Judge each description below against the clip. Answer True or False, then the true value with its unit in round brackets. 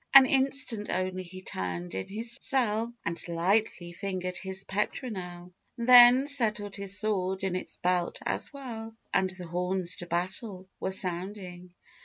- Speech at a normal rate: True (145 wpm)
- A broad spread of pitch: False (3.8 semitones)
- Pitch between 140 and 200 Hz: True (190 Hz)